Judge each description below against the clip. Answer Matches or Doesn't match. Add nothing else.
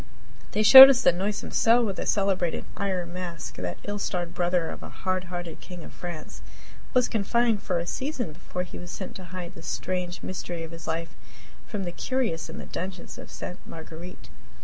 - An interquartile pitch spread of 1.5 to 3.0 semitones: Matches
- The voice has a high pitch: Doesn't match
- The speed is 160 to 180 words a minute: Doesn't match